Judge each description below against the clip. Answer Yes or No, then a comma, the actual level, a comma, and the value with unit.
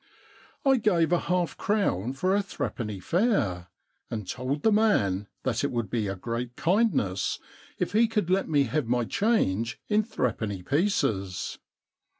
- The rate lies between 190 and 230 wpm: No, average, 155 wpm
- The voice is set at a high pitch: No, low, 135 Hz